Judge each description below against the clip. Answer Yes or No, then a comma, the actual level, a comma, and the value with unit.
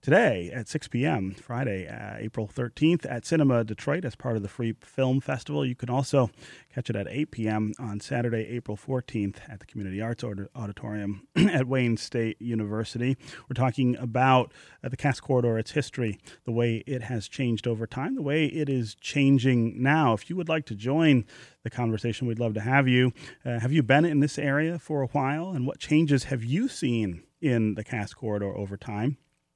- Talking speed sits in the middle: Yes, average, 195 wpm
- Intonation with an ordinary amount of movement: Yes, average, 3.7 semitones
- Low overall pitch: Yes, low, 125 Hz